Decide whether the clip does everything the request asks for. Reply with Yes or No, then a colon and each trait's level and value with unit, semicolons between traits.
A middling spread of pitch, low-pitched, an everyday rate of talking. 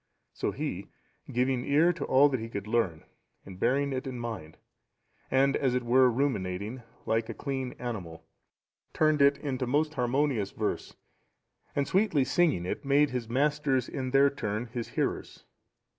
Yes: average, 3.5 semitones; low, 130 Hz; average, 160 wpm